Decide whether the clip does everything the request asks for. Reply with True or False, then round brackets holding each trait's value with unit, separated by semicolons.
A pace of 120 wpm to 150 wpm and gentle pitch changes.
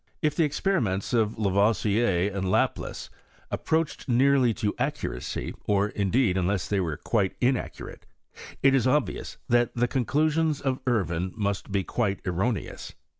False (140 wpm; 5.0 semitones)